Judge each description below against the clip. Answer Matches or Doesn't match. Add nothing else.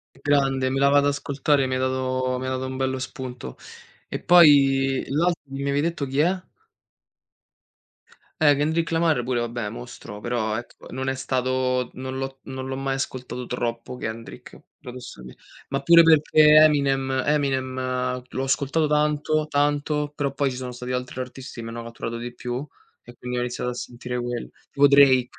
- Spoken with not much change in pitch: Matches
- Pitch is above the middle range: Doesn't match